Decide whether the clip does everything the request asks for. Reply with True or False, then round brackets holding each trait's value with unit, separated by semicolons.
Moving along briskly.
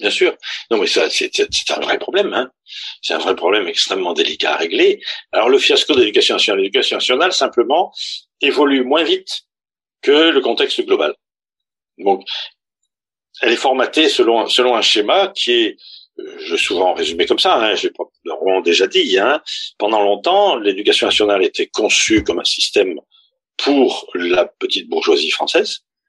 False (165 wpm)